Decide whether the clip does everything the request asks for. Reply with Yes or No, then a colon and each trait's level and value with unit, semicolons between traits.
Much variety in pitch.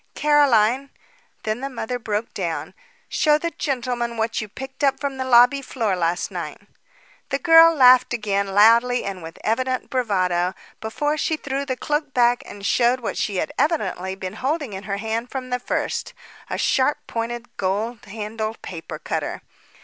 No: average, 4.4 semitones